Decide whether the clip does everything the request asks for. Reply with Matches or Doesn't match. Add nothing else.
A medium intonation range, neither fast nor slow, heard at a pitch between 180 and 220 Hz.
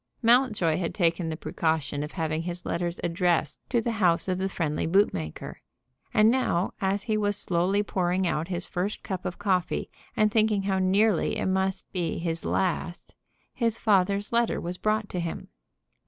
Matches